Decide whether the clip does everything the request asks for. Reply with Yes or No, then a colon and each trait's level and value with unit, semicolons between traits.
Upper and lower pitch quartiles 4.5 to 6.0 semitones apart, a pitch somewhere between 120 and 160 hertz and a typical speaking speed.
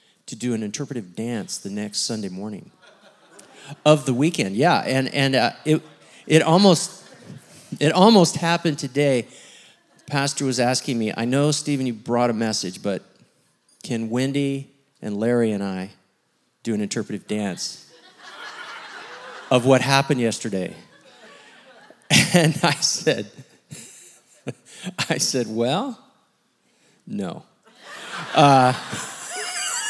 No: average, 4.9 semitones; low, 135 Hz; slow, 115 wpm